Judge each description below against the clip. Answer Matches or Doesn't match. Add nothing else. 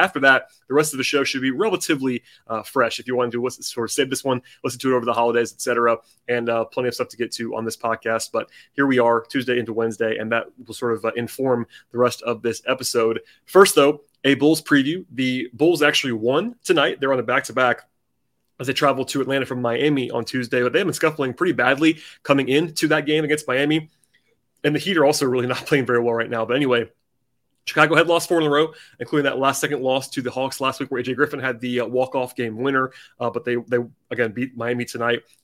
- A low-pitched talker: Matches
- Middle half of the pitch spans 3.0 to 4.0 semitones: Matches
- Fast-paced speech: Matches